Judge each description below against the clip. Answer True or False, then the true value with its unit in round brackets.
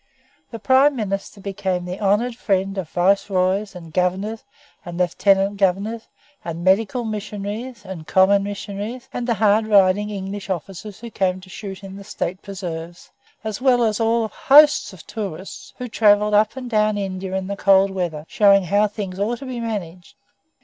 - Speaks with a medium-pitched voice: False (200 Hz)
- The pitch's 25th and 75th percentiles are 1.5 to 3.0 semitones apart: True (2.5 semitones)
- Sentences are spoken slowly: False (170 wpm)